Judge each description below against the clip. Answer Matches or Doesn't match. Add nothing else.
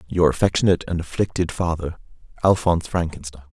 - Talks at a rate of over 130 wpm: Doesn't match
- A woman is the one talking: Doesn't match